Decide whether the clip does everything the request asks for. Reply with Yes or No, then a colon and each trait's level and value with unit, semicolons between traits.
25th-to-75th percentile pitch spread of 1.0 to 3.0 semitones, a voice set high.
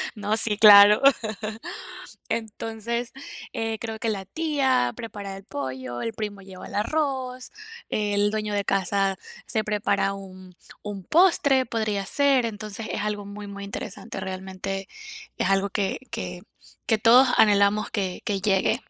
Yes: narrow, 2.5 semitones; high, 205 Hz